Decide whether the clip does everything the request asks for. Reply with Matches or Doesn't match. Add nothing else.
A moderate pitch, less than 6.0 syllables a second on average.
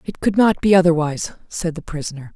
Doesn't match